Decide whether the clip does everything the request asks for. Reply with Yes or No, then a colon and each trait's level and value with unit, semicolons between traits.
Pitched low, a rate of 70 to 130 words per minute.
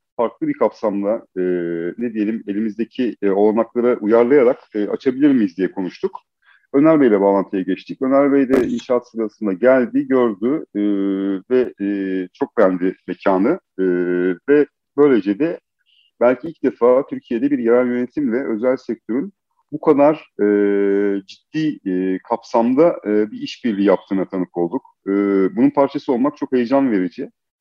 No: low, 115 Hz; fast, 140 wpm